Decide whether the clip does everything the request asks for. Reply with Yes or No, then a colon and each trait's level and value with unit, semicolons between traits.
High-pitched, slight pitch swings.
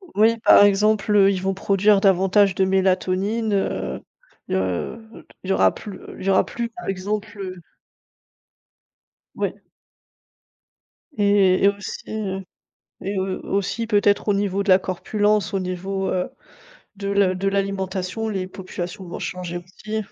Yes: high, 195 Hz; narrow, 1.8 semitones